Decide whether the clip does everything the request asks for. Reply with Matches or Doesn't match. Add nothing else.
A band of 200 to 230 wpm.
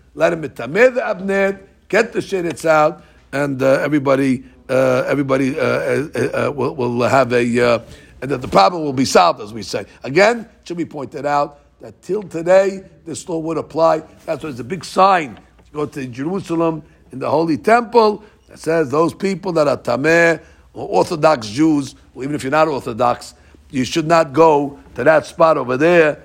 Doesn't match